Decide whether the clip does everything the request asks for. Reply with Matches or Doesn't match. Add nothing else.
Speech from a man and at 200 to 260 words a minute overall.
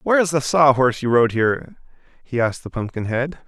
Matches